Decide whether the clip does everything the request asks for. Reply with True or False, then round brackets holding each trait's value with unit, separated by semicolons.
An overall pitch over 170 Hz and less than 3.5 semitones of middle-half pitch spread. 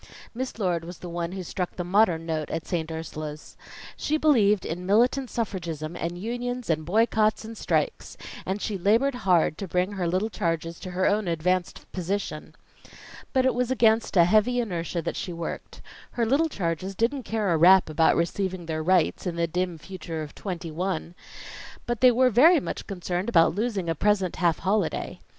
False (185 Hz; 4.6 semitones)